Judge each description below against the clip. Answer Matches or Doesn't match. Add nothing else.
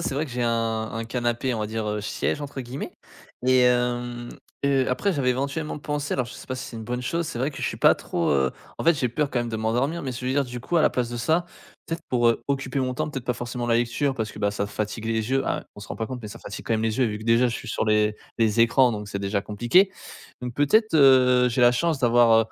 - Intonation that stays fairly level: Doesn't match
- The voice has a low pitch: Matches